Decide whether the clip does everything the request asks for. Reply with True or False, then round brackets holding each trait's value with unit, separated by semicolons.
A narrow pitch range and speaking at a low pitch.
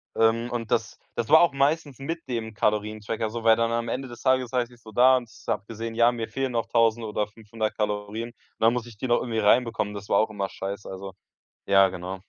True (2.2 semitones; 115 Hz)